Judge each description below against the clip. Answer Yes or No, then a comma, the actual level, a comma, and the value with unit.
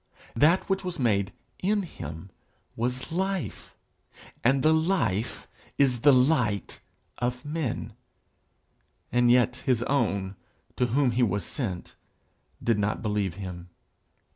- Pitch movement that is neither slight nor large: No, wide, 6.0 semitones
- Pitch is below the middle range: Yes, low, 125 Hz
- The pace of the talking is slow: Yes, slow, 120 wpm